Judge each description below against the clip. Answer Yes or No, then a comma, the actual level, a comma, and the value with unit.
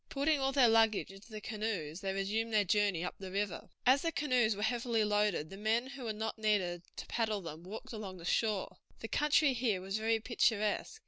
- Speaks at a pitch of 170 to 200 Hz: No, high, 215 Hz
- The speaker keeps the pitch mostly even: No, average, 3.1 semitones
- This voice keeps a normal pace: No, fast, 210 wpm